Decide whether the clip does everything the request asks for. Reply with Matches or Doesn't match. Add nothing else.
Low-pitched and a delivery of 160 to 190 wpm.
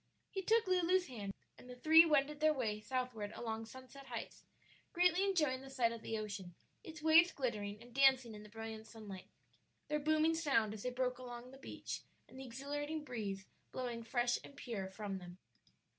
Doesn't match